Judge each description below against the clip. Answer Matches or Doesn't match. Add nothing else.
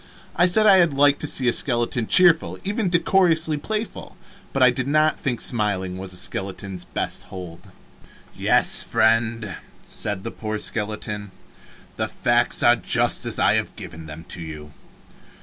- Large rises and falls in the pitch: Matches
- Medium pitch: Doesn't match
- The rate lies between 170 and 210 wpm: Doesn't match